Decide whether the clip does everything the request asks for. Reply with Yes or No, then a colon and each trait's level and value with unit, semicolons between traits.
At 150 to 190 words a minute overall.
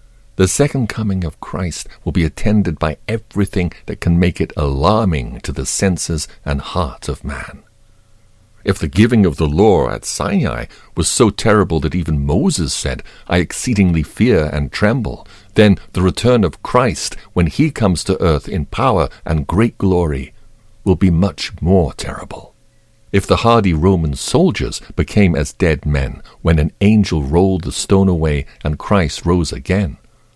Yes: average, 160 wpm